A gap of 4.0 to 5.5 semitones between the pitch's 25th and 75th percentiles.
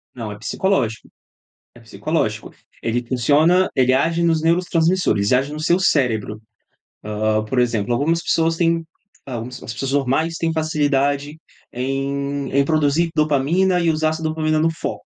Yes: average, 4.6 semitones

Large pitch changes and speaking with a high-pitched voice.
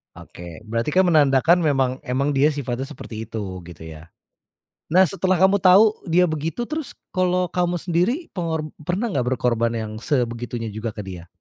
No: wide, 7.6 semitones; medium, 145 Hz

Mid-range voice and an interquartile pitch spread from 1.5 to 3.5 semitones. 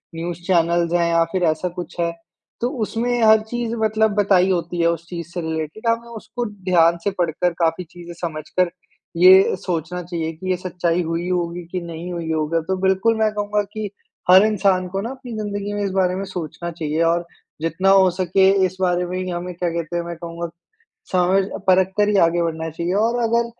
Yes: medium, 180 Hz; average, 2.8 semitones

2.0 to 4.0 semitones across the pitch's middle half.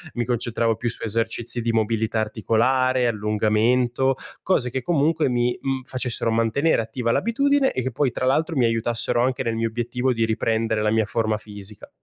Yes: narrow, 2.5 semitones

